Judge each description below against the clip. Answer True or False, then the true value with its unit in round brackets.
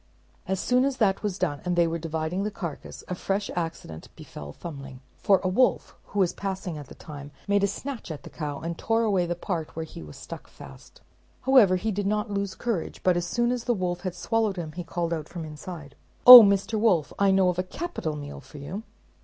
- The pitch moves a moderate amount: True (4.0 semitones)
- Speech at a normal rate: False (230 wpm)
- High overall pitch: False (180 Hz)